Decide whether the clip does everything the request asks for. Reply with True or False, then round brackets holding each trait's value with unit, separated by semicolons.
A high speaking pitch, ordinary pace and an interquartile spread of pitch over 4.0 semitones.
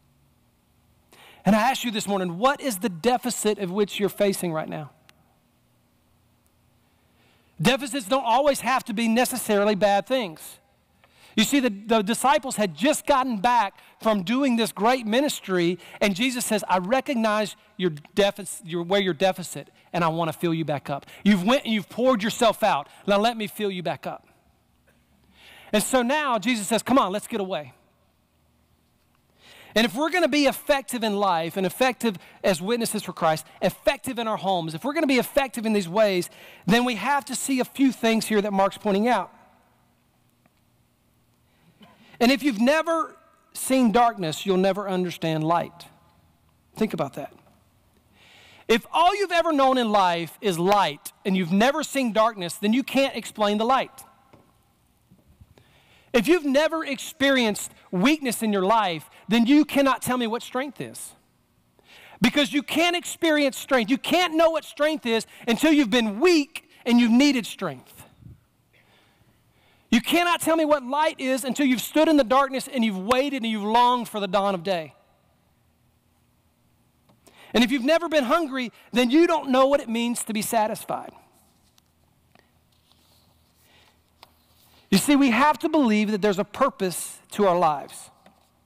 True (230 Hz; 165 wpm; 5.3 semitones)